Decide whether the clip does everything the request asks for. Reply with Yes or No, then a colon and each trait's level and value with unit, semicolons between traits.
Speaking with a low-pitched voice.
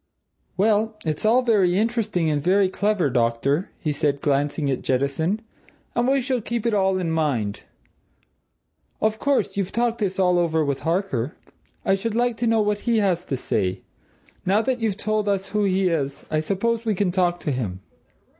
No: high, 190 Hz